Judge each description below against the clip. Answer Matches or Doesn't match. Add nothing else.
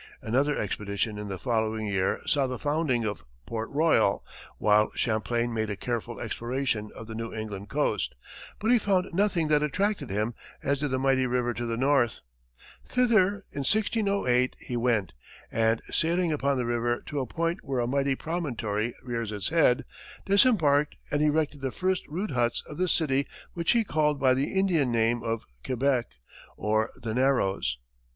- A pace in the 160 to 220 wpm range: Matches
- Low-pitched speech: Matches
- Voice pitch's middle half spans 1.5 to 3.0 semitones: Doesn't match